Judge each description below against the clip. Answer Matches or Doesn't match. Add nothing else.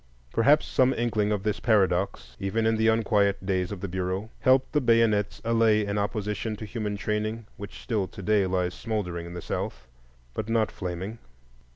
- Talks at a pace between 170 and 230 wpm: Matches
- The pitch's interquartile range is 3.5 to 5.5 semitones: Doesn't match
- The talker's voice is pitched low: Matches